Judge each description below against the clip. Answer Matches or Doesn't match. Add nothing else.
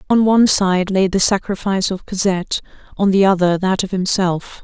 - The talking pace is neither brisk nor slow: Matches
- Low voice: Doesn't match